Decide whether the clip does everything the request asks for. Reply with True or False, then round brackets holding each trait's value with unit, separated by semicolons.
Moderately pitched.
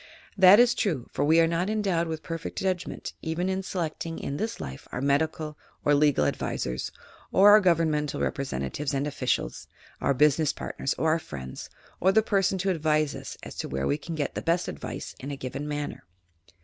True (155 Hz)